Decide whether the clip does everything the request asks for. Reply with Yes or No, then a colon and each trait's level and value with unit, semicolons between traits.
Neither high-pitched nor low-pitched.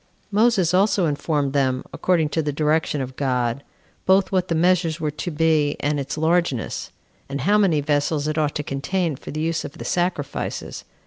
Yes: medium, 155 Hz